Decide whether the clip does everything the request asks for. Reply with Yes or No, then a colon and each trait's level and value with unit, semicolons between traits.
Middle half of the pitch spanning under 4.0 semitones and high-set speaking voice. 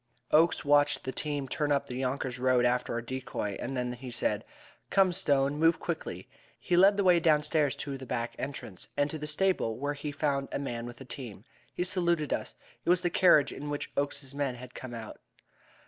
No: average, 3.4 semitones; medium, 140 Hz